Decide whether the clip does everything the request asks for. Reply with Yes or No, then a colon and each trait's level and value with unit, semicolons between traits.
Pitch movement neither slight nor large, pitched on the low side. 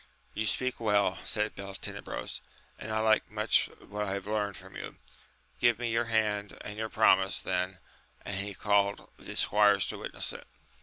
No: narrow, 1.6 semitones; low, 105 Hz